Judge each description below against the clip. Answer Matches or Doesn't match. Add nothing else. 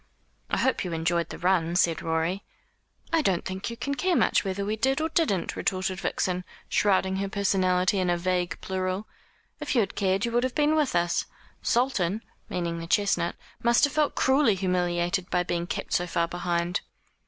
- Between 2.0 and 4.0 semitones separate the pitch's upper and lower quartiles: Doesn't match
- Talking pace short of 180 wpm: Doesn't match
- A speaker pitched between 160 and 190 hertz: Matches